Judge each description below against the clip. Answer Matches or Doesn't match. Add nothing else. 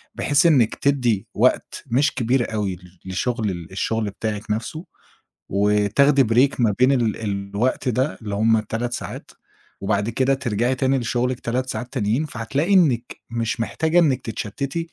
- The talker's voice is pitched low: Matches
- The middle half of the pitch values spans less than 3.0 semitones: Doesn't match